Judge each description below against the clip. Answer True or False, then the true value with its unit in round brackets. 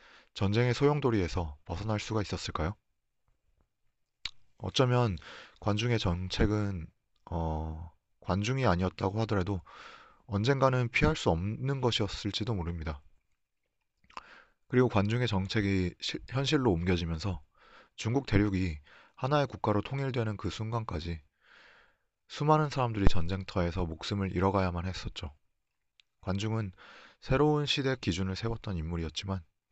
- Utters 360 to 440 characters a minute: False (285 characters per minute)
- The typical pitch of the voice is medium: False (100 Hz)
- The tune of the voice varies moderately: True (4.9 semitones)